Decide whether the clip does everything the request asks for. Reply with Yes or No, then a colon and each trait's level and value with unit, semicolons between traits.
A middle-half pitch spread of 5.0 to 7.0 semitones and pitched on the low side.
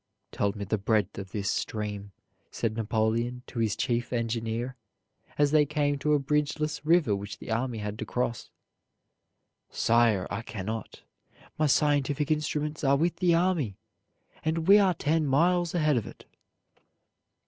Yes: wide, 5.5 semitones; low, 130 Hz